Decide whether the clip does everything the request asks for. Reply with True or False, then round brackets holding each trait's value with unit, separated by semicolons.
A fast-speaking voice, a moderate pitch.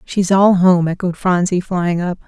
False (185 wpm; 180 Hz)